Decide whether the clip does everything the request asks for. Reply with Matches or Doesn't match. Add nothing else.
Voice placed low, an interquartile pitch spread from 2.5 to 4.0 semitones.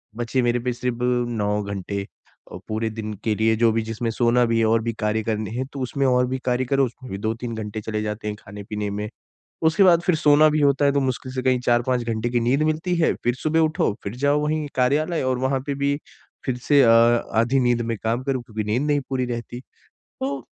Matches